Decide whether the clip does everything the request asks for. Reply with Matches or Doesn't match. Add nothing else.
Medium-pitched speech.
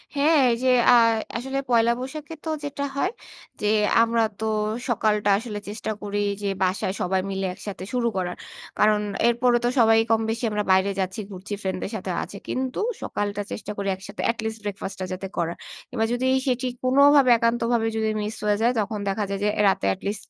Doesn't match